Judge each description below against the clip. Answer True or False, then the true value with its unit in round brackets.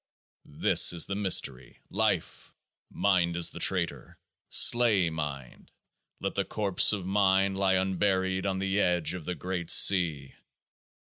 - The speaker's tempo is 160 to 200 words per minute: False (135 wpm)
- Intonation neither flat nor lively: False (2.1 semitones)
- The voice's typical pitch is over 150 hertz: False (95 Hz)